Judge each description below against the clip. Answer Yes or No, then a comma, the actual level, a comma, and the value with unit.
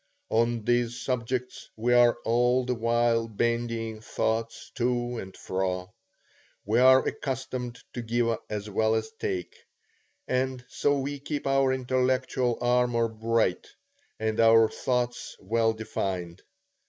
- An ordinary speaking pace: No, slow, 125 wpm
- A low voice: Yes, low, 120 Hz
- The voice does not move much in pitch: Yes, narrow, 2.0 semitones